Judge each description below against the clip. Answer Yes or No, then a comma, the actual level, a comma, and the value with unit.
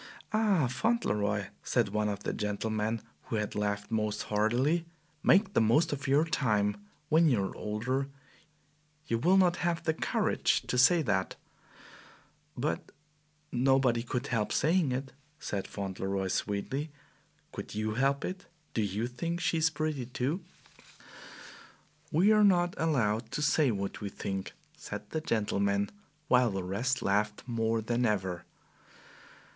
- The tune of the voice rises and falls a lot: Yes, wide, 6.8 semitones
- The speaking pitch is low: Yes, low, 120 Hz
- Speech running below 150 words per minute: Yes, average, 140 wpm